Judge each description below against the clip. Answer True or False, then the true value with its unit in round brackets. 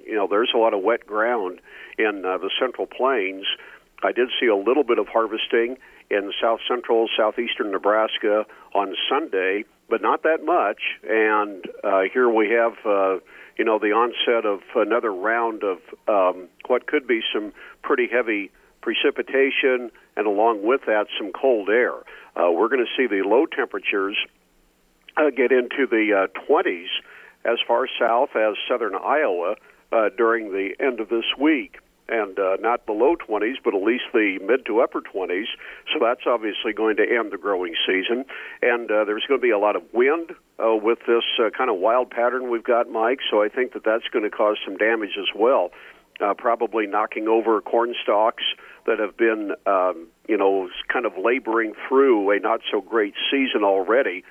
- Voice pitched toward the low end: True (115 Hz)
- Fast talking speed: False (180 wpm)